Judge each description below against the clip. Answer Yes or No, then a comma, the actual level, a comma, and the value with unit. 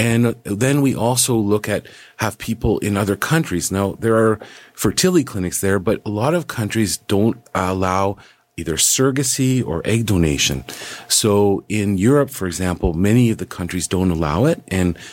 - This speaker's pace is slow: No, average, 165 wpm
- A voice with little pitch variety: No, average, 3.9 semitones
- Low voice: Yes, low, 105 Hz